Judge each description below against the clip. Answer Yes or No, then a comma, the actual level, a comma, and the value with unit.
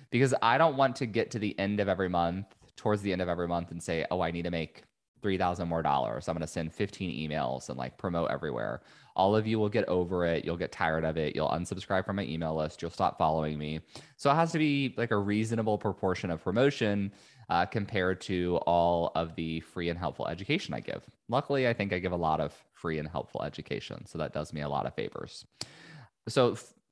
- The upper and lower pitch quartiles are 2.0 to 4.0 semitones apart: No, average, 4.6 semitones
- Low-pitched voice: Yes, very low, 90 Hz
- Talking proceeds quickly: Yes, fast, 235 wpm